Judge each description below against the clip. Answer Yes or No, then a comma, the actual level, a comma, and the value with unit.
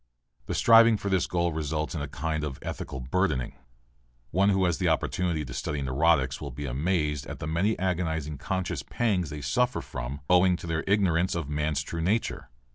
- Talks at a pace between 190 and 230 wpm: Yes, average, 195 wpm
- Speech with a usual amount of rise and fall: Yes, average, 3.9 semitones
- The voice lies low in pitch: Yes, very low, 80 Hz